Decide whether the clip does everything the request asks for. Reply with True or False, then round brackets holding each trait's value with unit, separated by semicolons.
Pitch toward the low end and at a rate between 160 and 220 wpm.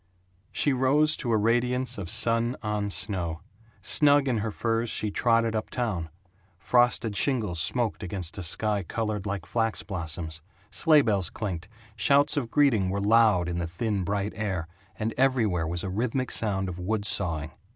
True (105 Hz; 165 wpm)